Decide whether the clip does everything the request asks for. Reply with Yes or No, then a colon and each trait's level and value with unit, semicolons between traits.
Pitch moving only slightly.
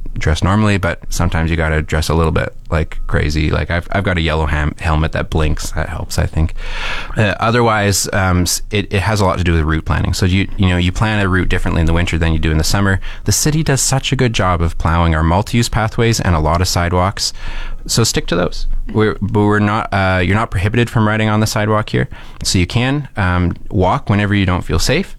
No: average, 4.4 semitones